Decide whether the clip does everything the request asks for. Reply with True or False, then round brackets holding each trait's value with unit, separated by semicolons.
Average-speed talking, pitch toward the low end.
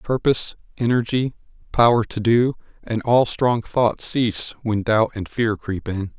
True (155 wpm; 115 Hz)